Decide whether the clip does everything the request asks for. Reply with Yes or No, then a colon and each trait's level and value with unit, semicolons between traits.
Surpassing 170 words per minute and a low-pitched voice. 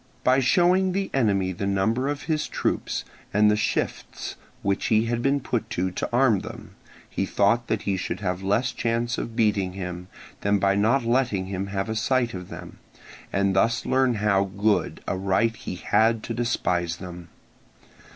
Yes: average, 180 wpm; low, 105 Hz